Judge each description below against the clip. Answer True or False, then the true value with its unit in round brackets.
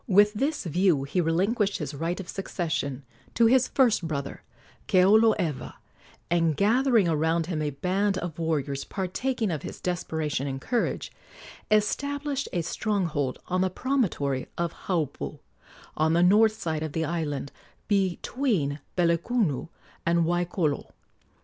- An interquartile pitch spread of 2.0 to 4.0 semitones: False (4.9 semitones)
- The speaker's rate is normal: False (130 wpm)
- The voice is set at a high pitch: False (175 Hz)